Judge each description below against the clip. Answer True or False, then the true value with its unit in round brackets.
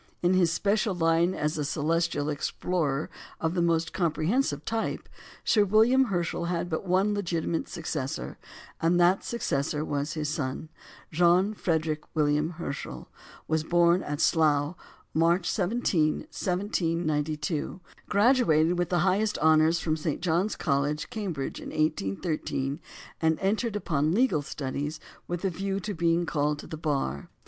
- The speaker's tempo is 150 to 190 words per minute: False (140 wpm)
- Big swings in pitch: False (3.3 semitones)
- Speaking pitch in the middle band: True (165 Hz)